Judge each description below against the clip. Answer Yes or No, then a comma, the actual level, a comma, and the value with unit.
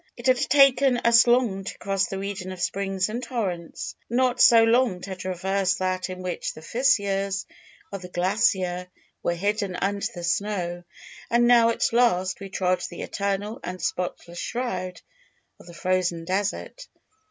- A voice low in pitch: No, high, 195 Hz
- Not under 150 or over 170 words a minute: Yes, average, 160 wpm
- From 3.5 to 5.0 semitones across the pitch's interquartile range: Yes, average, 4.1 semitones